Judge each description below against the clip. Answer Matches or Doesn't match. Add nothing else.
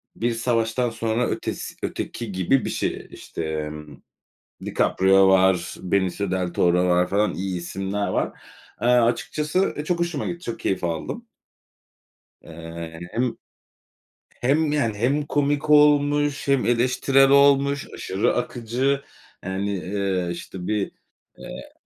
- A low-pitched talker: Matches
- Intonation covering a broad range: Matches